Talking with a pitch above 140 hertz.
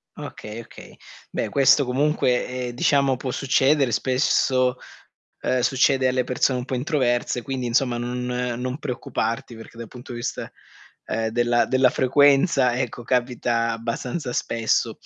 No: low, 125 Hz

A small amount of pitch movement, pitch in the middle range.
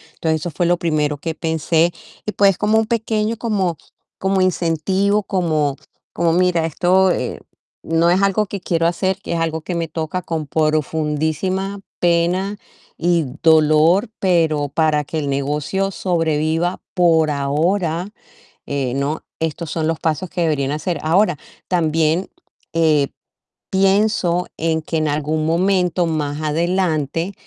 No: average, 3.1 semitones; medium, 165 Hz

